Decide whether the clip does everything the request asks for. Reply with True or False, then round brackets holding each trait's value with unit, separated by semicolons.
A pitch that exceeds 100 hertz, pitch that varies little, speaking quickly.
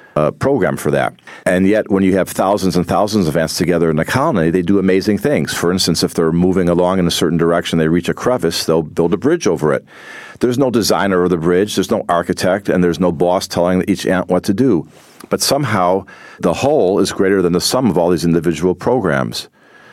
False (90 Hz; 1.8 semitones; 230 wpm)